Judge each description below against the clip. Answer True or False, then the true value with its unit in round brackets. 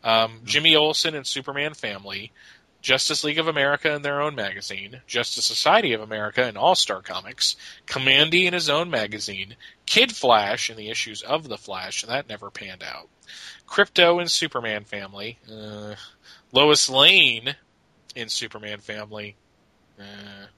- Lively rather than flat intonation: True (6.1 semitones)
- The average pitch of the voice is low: True (120 Hz)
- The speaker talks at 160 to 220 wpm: False (145 wpm)